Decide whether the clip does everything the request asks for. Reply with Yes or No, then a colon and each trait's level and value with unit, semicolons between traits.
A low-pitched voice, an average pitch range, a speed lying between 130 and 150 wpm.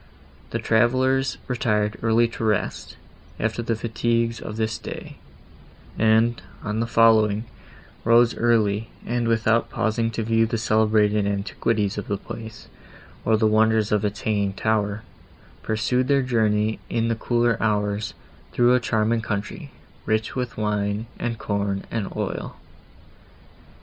No: low, 110 Hz; narrow, 1.7 semitones; slow, 135 wpm